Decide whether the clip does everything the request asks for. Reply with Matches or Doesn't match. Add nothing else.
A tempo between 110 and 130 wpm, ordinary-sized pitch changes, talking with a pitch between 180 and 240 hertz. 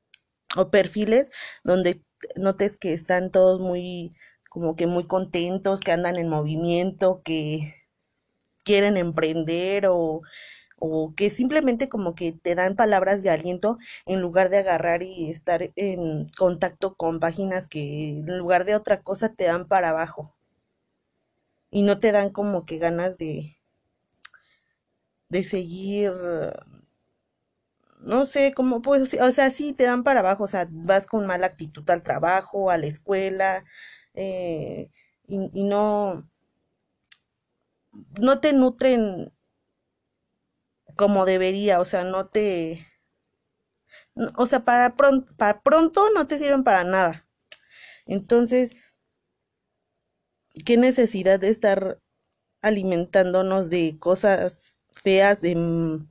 Matches